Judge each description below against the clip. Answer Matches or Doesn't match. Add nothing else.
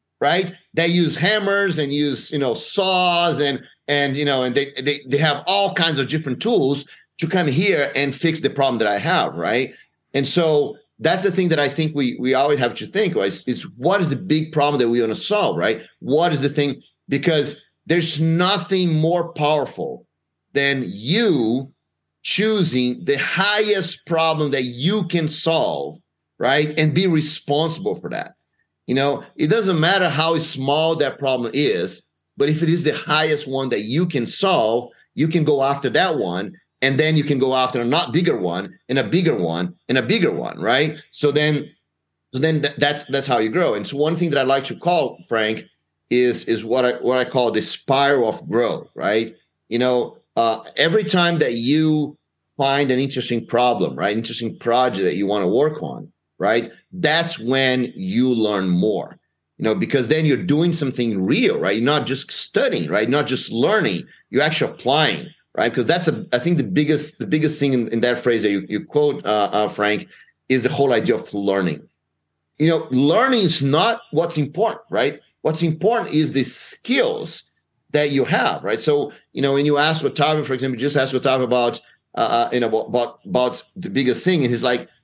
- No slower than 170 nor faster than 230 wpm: Matches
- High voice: Doesn't match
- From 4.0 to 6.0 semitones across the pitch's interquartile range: Matches